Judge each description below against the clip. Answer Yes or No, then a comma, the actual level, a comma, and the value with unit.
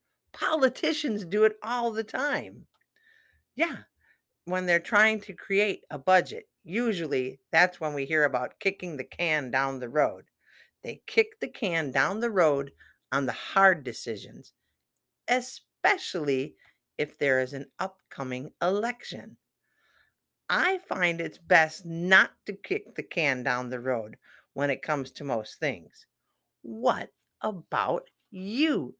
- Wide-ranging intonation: Yes, wide, 8.3 semitones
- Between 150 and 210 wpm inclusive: No, slow, 135 wpm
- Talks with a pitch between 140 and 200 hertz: Yes, medium, 185 Hz